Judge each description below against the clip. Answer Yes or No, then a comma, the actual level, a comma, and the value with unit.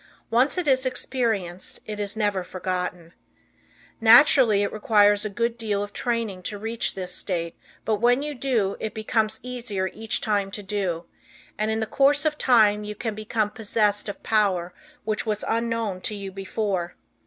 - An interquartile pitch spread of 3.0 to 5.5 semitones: No, narrow, 2.6 semitones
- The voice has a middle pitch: No, high, 215 Hz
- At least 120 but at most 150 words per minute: No, average, 170 wpm